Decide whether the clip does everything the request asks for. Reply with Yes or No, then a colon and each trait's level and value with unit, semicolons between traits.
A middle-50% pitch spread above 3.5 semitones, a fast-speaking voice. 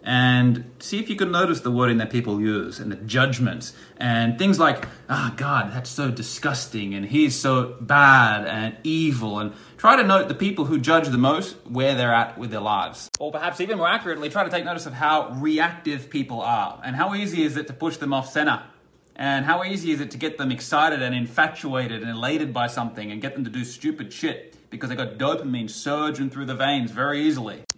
Yes: average, 4.5 semitones; fast, 220 wpm